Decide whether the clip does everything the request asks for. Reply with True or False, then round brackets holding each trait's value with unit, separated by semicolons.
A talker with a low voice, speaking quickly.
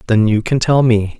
True (115 Hz; 250 wpm)